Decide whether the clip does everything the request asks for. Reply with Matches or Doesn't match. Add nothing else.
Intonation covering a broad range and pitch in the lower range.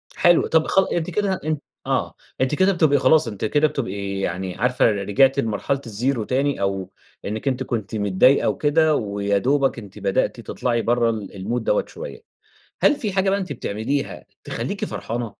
Matches